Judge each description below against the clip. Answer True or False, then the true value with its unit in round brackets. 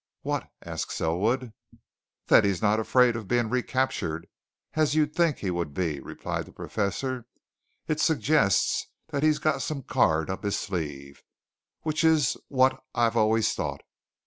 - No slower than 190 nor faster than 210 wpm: False (145 wpm)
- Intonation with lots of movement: True (6.9 semitones)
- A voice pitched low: True (115 Hz)